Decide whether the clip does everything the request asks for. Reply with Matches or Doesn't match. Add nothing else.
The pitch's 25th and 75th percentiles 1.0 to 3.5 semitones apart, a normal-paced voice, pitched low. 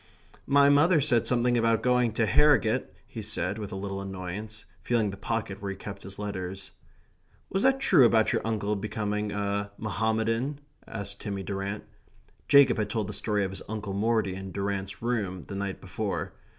Matches